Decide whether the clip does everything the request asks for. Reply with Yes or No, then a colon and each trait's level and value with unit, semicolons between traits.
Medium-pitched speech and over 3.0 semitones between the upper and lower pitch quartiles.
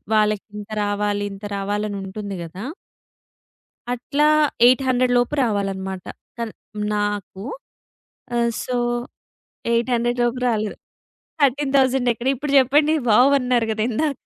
No: high, 235 Hz; average, 3.7 semitones